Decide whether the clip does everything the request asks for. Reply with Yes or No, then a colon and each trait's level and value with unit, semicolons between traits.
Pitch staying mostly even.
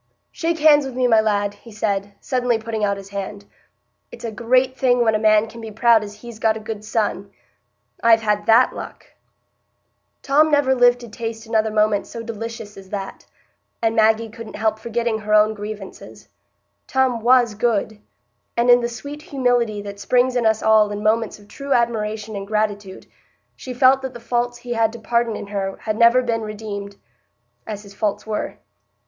Yes: narrow, 2.3 semitones